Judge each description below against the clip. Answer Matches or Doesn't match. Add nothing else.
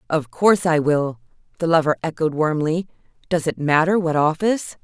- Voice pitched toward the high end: Doesn't match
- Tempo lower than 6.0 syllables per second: Matches